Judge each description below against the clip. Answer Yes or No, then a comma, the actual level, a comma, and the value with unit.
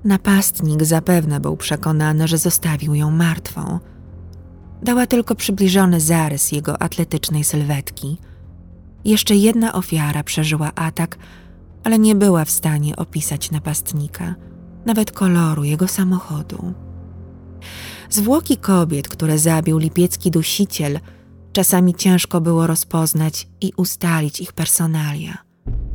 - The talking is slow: Yes, slow, 105 wpm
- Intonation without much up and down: No, average, 3.7 semitones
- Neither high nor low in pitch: Yes, medium, 160 Hz